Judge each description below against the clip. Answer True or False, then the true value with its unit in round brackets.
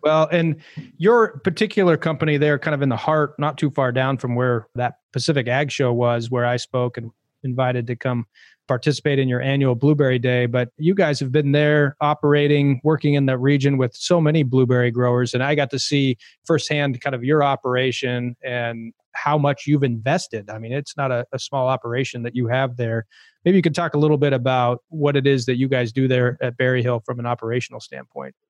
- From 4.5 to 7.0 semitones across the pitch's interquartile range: False (3.1 semitones)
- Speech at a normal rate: False (215 wpm)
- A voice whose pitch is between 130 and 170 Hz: True (135 Hz)